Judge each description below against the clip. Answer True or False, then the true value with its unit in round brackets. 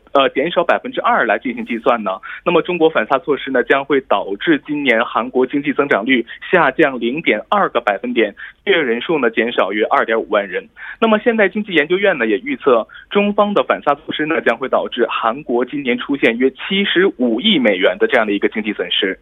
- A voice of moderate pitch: False (215 Hz)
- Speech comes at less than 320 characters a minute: False (330 characters per minute)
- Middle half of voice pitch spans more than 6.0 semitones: True (8.4 semitones)